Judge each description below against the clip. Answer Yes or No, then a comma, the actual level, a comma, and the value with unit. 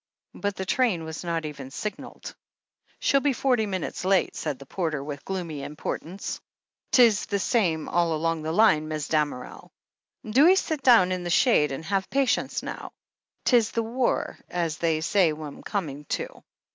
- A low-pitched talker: No, medium, 175 Hz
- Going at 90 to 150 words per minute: No, average, 170 wpm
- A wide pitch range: Yes, wide, 5.8 semitones